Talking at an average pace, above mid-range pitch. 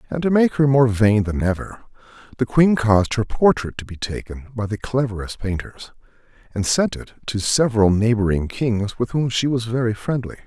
No: average, 190 wpm; low, 115 Hz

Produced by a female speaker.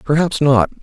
No: male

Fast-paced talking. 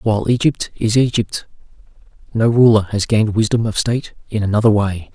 No: average, 165 wpm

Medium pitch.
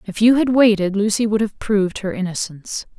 No: high, 205 Hz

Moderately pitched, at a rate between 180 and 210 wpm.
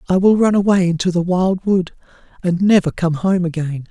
Yes: medium, 180 Hz; average, 200 wpm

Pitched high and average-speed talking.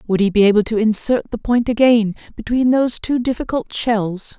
Yes: high, 225 Hz; average, 190 wpm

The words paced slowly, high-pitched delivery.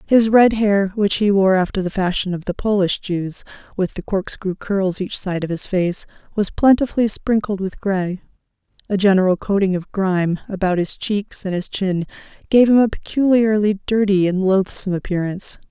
No: average, 170 wpm; high, 195 Hz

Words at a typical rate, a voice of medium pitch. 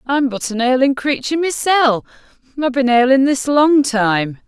No: average, 150 wpm; very high, 260 Hz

